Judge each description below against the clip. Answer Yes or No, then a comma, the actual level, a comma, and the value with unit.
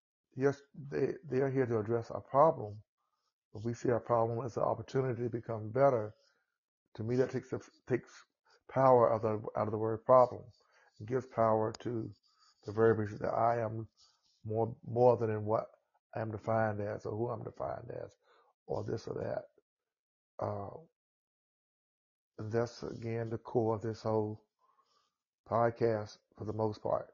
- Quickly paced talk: No, average, 165 wpm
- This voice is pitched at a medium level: No, low, 115 Hz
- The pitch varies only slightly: Yes, narrow, 1.9 semitones